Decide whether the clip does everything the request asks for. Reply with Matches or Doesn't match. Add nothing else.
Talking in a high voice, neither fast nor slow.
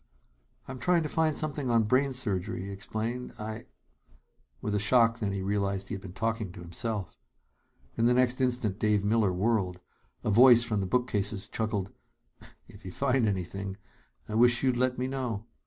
Doesn't match